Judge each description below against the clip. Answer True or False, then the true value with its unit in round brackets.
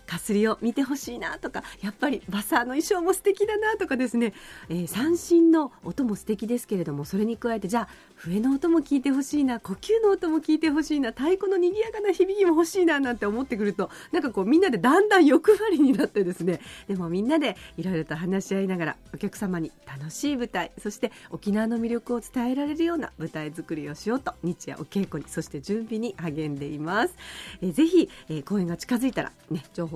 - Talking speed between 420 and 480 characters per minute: True (430 characters per minute)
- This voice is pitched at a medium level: False (235 Hz)